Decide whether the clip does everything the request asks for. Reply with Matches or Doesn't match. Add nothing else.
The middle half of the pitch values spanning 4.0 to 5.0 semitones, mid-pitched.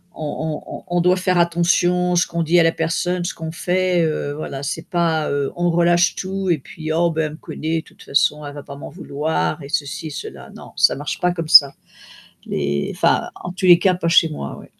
Doesn't match